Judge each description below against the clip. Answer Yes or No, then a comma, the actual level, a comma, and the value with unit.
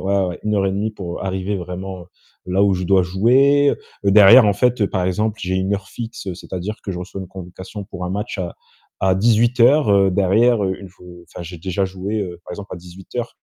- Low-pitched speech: Yes, very low, 95 Hz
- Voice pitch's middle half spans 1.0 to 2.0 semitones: No, narrow, 2.5 semitones